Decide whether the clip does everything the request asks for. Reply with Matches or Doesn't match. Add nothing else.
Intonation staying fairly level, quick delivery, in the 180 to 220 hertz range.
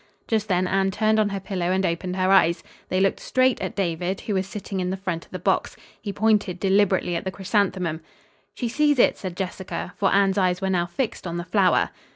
Matches